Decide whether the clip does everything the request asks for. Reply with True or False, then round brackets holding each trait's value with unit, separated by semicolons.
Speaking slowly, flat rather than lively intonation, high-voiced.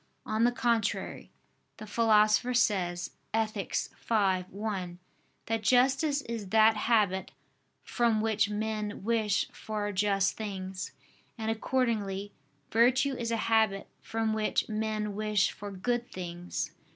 True (120 wpm; 2.2 semitones; 215 Hz)